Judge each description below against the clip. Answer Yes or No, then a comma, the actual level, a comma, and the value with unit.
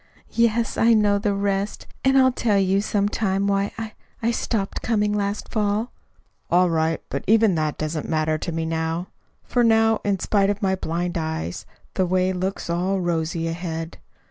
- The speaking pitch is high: Yes, high, 195 Hz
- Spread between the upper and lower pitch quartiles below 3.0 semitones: No, average, 4.1 semitones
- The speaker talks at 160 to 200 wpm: Yes, average, 175 wpm